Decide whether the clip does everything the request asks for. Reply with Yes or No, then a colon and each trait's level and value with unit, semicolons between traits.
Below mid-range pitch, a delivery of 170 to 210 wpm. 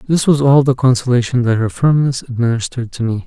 Yes: low, 125 Hz; average, 200 wpm